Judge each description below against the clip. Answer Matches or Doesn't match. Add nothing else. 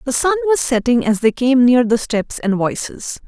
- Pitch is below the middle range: Doesn't match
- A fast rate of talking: Matches